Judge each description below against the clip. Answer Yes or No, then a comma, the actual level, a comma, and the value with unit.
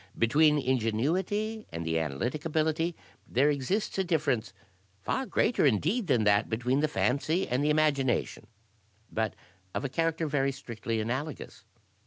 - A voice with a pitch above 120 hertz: Yes, medium, 140 Hz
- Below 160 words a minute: Yes, average, 140 wpm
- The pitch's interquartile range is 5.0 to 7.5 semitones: Yes, wide, 5.4 semitones